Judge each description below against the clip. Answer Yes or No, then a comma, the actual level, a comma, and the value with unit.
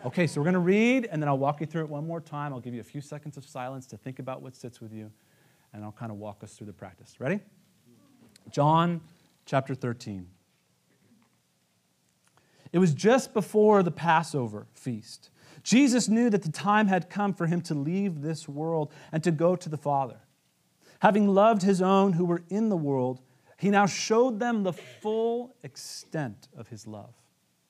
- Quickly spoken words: No, average, 195 wpm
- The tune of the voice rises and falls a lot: Yes, wide, 6.9 semitones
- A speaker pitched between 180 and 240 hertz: No, medium, 155 Hz